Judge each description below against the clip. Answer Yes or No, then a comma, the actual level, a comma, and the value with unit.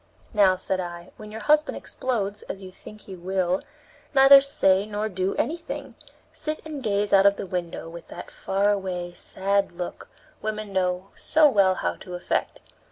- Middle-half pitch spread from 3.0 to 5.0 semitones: No, narrow, 2.5 semitones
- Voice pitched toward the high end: Yes, high, 195 Hz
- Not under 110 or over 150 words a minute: No, average, 170 wpm